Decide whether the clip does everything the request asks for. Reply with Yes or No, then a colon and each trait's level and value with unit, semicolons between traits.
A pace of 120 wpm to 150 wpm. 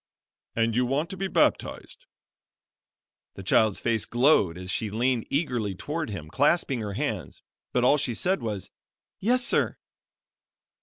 Yes: average, 145 wpm